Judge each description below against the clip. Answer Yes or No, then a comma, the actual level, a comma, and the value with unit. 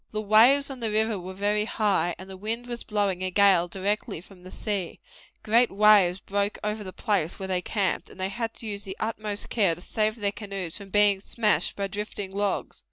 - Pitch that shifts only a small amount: Yes, narrow, 2.1 semitones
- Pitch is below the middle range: No, high, 205 Hz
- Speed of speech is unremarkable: No, fast, 215 wpm